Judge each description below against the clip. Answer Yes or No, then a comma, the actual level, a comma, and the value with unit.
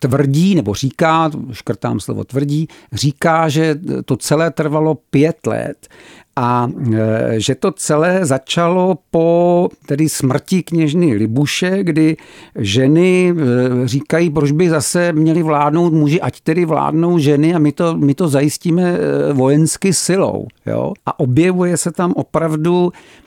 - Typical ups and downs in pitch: Yes, average, 3.6 semitones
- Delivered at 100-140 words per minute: Yes, average, 130 wpm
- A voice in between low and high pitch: Yes, medium, 155 Hz